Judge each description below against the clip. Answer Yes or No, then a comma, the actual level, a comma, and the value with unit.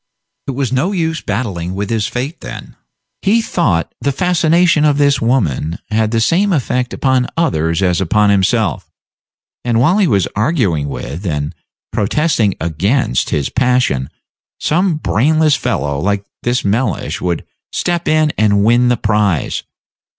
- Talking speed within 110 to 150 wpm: Yes, average, 145 wpm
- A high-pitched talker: No, low, 120 Hz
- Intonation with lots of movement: Yes, wide, 7.6 semitones